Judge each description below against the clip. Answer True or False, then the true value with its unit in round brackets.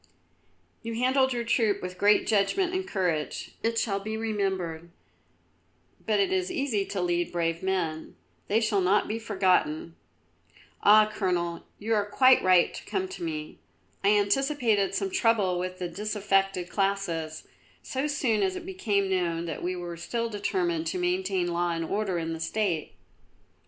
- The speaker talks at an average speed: True (160 wpm)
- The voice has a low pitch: False (195 Hz)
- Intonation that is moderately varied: True (4.4 semitones)